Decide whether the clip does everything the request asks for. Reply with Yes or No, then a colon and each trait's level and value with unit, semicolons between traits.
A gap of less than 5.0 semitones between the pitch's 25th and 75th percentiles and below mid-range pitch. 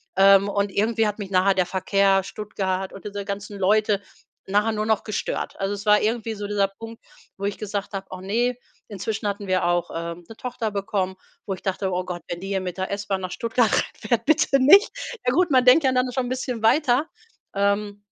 No: narrow, 2.6 semitones; high, 205 Hz